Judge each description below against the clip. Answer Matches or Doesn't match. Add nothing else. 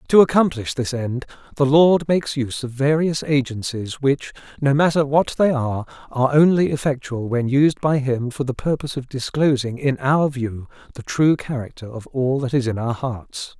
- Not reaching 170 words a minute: Doesn't match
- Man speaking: Matches